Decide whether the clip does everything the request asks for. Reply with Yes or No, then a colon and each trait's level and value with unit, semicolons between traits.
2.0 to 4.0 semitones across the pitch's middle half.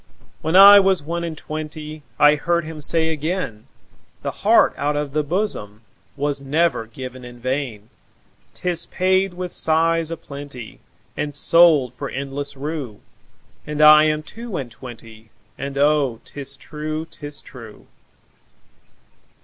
Yes: average, 3.3 semitones